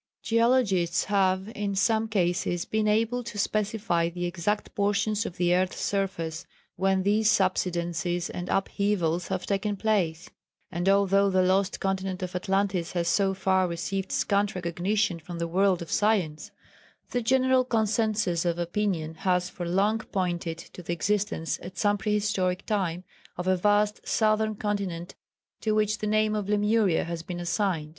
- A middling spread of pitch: Yes, average, 3.1 semitones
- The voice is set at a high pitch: Yes, high, 195 Hz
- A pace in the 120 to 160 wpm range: Yes, average, 155 wpm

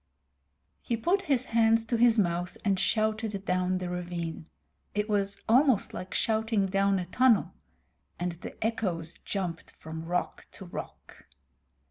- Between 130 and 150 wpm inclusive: Yes, average, 140 wpm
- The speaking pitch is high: Yes, high, 200 Hz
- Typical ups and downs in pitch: Yes, average, 4.0 semitones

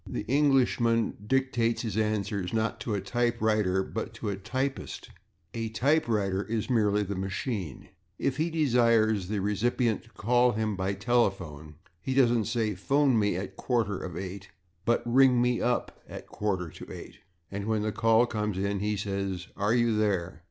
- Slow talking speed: No, average, 170 wpm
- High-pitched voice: No, low, 110 Hz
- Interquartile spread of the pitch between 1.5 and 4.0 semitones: Yes, average, 3.4 semitones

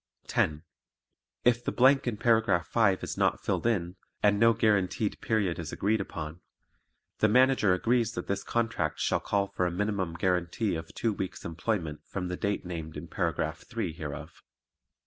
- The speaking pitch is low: Yes, low, 100 Hz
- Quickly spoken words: No, average, 165 wpm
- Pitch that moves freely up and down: No, average, 4.6 semitones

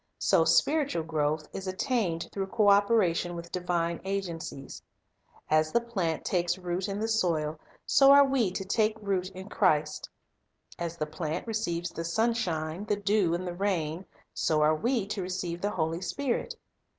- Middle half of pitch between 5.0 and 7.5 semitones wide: No, average, 3.9 semitones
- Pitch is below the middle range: No, medium, 180 Hz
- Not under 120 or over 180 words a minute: Yes, average, 165 wpm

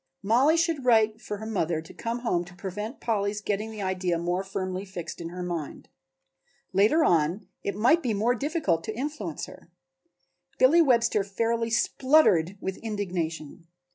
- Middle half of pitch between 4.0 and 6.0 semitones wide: Yes, average, 4.6 semitones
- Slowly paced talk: No, average, 160 wpm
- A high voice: Yes, high, 205 Hz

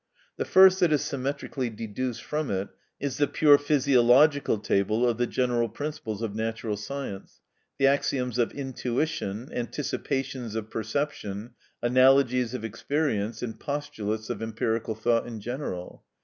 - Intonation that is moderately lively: Yes, average, 4.1 semitones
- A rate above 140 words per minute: No, slow, 135 wpm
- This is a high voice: No, low, 120 Hz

